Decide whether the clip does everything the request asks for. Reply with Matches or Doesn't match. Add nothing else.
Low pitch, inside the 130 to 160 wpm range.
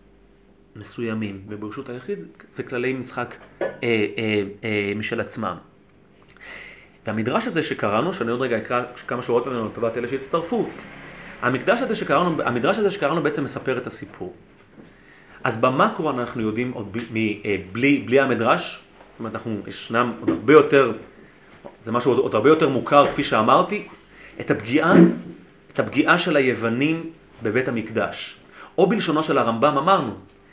Matches